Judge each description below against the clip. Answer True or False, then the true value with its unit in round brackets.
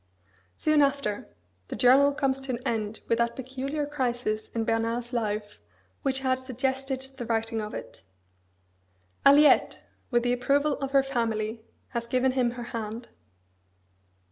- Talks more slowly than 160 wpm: True (140 wpm)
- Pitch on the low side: False (245 Hz)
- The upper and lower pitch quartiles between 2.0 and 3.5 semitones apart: True (2.9 semitones)